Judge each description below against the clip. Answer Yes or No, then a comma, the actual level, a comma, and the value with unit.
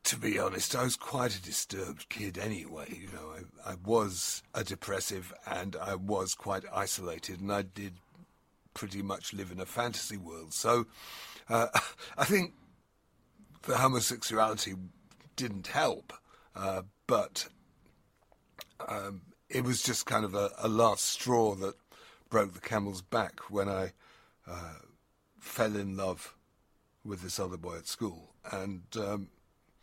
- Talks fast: No, average, 145 wpm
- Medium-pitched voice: No, low, 100 Hz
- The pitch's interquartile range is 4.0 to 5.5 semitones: No, average, 3.4 semitones